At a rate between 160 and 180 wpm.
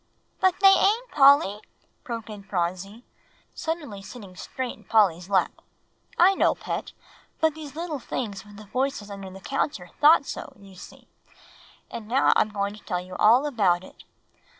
Yes: average, 170 wpm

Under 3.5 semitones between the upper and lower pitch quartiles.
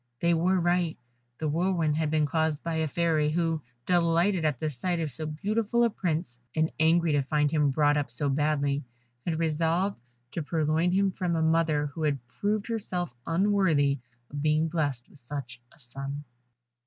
Yes: average, 2.8 semitones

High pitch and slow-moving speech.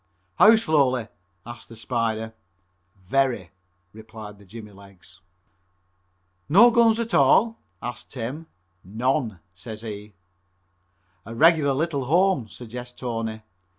No: low, 120 Hz; slow, 110 wpm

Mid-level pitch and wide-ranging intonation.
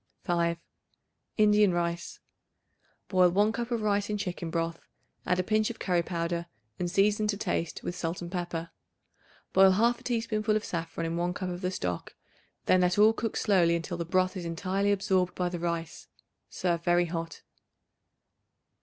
No: medium, 180 Hz; average, 3.3 semitones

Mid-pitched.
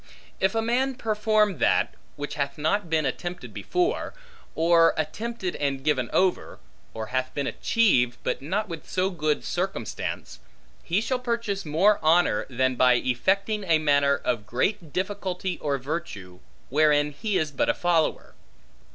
Yes: medium, 165 Hz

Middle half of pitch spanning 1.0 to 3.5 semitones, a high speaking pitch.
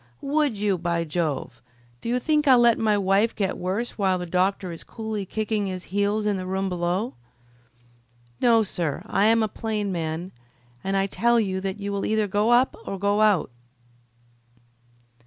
Yes: average, 2.9 semitones; high, 200 Hz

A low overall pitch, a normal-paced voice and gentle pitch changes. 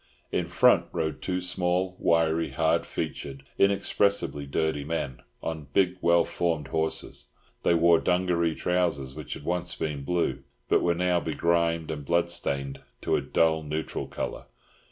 Yes: very low, 85 Hz; average, 145 wpm; narrow, 2.3 semitones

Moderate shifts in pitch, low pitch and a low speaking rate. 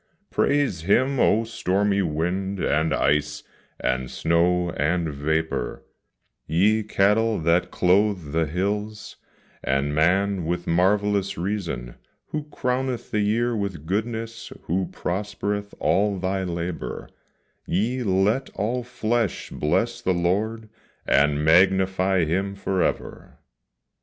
Yes: average, 3.9 semitones; very low, 95 Hz; slow, 110 wpm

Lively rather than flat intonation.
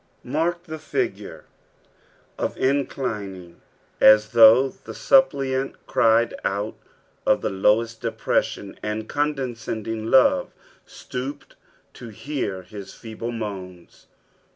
No: average, 4.1 semitones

